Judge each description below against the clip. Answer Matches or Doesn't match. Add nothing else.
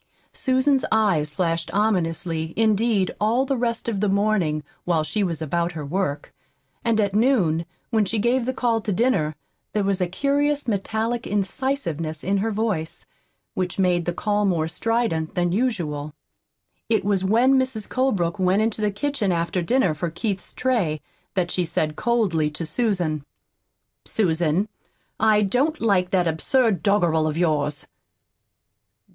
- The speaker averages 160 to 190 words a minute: Doesn't match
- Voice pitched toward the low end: Doesn't match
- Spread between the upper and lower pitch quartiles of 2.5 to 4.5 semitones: Doesn't match